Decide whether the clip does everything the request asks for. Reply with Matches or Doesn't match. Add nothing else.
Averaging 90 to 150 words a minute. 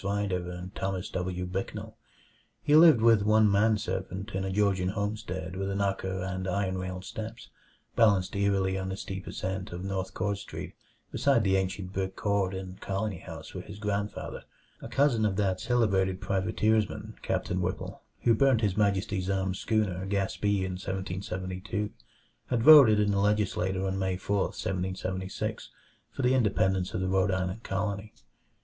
Doesn't match